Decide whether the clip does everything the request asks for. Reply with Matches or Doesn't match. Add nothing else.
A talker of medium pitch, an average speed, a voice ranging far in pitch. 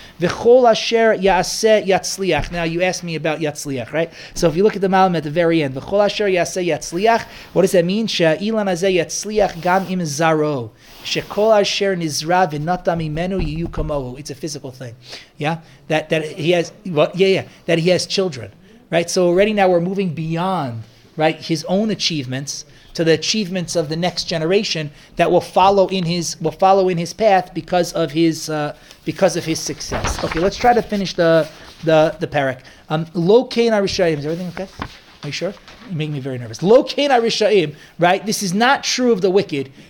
Doesn't match